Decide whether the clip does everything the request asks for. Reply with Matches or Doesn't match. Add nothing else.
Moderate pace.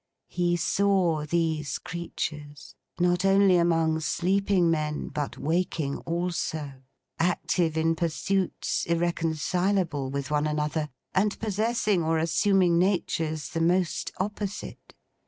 Doesn't match